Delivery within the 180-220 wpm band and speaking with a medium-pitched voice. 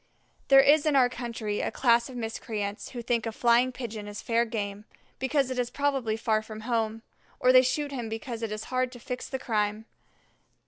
No: average, 200 wpm; high, 235 Hz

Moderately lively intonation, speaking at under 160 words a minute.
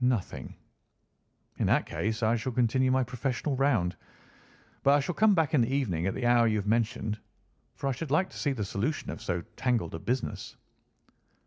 No: average, 3.9 semitones; average, 195 wpm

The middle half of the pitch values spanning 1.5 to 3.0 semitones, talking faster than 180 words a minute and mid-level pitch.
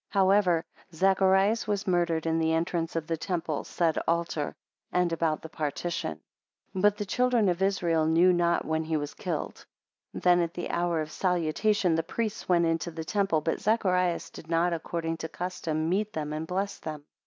Yes: narrow, 2.6 semitones; average, 190 wpm; medium, 170 Hz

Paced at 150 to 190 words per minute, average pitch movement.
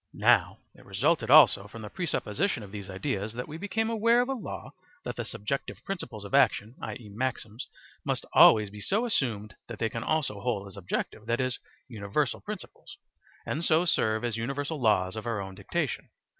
No: average, 185 wpm; wide, 6.8 semitones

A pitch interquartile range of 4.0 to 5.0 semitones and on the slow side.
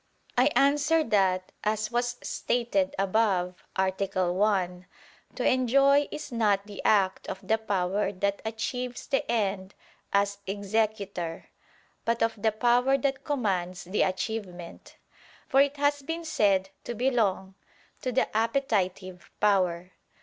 Yes: average, 4.5 semitones; slow, 130 wpm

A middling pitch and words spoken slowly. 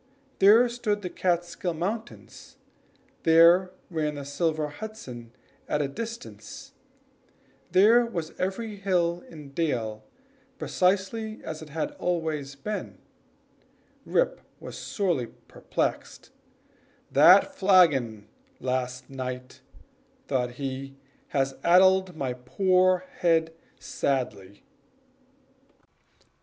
Yes: medium, 165 Hz; slow, 95 wpm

